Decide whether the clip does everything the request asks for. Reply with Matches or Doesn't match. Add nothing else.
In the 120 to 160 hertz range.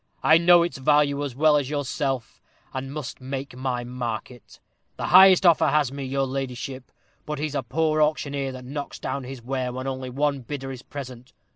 Matches